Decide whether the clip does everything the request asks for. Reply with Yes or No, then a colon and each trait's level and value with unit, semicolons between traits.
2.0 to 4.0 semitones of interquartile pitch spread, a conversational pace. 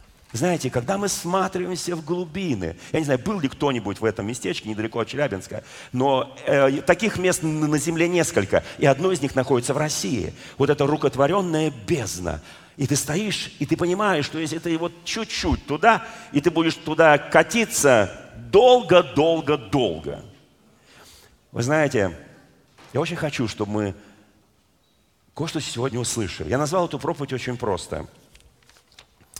No: wide, 5.5 semitones; average, 145 wpm